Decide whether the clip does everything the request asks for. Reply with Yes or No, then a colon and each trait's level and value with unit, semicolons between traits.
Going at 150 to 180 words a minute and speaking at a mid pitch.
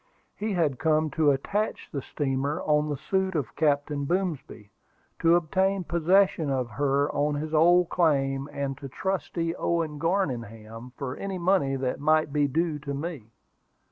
Yes: average, 155 wpm; medium, 150 Hz